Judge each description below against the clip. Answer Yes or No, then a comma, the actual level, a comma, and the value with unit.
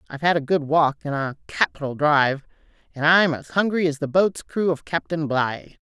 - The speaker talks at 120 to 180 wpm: No, fast, 205 wpm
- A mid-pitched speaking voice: Yes, medium, 155 Hz